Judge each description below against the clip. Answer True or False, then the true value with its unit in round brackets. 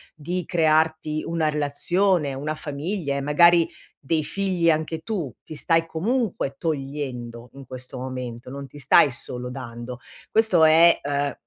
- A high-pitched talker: False (150 Hz)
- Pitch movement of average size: True (3.8 semitones)